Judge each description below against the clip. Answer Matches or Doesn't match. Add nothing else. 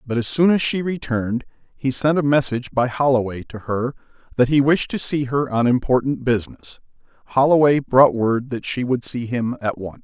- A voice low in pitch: Matches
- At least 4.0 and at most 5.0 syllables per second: Doesn't match